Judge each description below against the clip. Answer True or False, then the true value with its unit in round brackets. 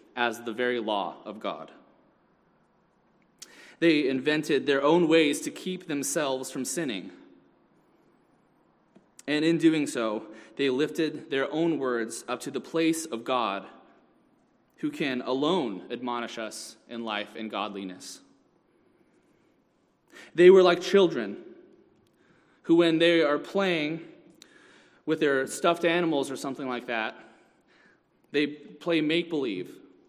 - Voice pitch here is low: False (145 Hz)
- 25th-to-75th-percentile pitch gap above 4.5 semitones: True (5.5 semitones)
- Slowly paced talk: True (120 wpm)